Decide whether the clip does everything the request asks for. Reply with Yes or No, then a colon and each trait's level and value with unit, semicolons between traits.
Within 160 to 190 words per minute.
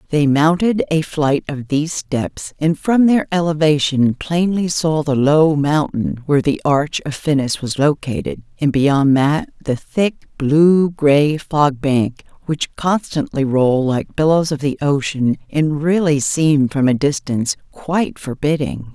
No: average, 150 wpm